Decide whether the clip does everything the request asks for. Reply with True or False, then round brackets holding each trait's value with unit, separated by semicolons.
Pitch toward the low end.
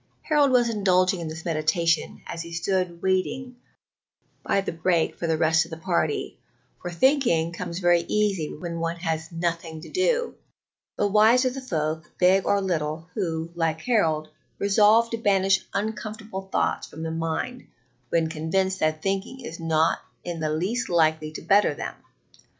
False (175 Hz)